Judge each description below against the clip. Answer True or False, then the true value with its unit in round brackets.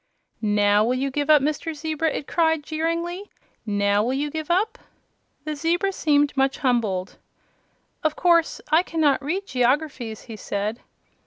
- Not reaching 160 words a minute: True (150 wpm)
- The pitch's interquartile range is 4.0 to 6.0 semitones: True (5.1 semitones)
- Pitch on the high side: True (290 Hz)